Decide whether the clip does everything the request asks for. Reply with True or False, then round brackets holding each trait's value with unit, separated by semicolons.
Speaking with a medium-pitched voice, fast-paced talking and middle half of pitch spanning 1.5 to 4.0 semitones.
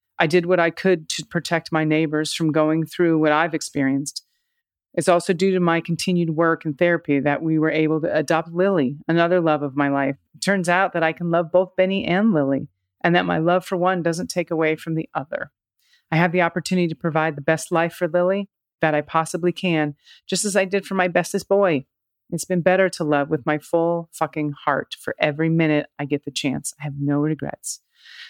True (165 Hz; 220 wpm; 2.7 semitones)